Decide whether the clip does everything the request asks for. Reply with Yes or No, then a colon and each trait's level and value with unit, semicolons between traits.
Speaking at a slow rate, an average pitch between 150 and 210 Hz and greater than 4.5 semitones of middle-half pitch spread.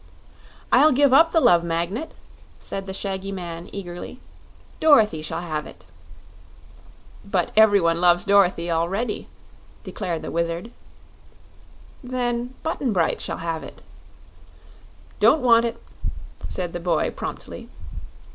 Yes: slow, 120 wpm; high, 190 Hz; wide, 5.6 semitones